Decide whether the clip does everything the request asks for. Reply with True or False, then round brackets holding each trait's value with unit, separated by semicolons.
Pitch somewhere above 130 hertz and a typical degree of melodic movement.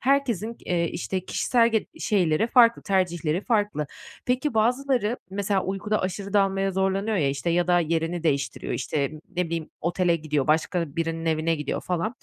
True (185 Hz; 4.5 semitones)